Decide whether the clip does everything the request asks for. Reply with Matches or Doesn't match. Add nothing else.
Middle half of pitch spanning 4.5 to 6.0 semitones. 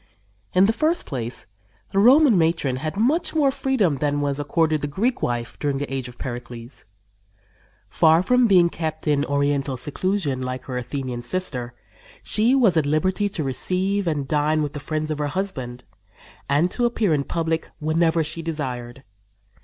Matches